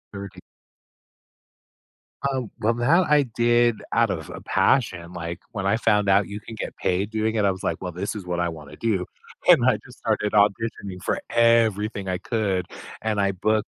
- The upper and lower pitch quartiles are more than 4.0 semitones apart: No, average, 3.3 semitones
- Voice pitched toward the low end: Yes, low, 105 Hz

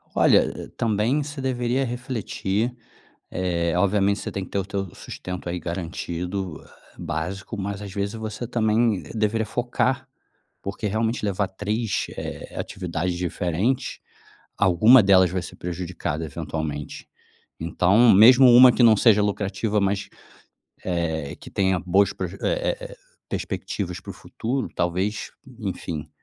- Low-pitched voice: Yes, low, 100 Hz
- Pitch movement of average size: Yes, average, 4.1 semitones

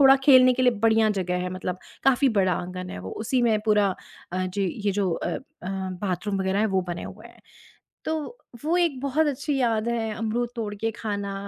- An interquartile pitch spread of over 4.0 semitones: Yes, average, 4.7 semitones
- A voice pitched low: No, high, 215 Hz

